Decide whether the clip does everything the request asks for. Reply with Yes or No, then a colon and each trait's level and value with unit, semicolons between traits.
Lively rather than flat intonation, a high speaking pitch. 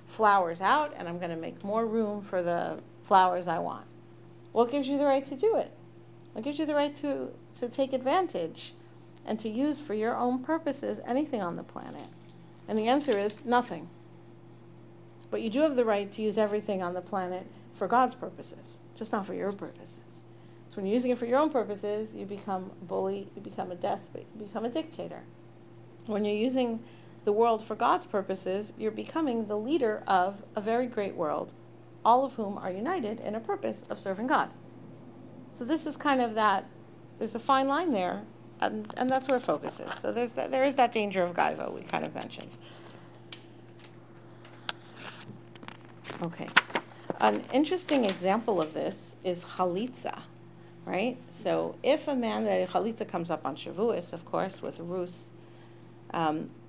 Yes: wide, 7.2 semitones; high, 205 Hz